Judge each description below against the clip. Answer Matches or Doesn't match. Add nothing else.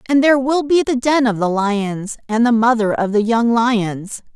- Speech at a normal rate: Doesn't match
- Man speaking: Doesn't match